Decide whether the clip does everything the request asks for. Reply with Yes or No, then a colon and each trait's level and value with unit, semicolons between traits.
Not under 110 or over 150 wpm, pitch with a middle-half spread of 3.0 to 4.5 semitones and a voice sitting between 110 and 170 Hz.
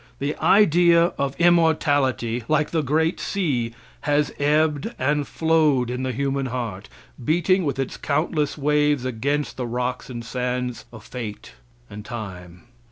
Yes: average, 140 wpm; average, 3.8 semitones; medium, 140 Hz